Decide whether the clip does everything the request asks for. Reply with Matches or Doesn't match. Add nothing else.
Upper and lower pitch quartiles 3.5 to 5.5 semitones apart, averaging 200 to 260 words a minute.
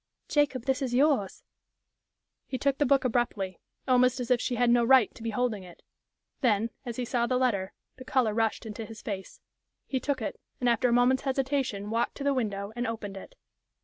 Doesn't match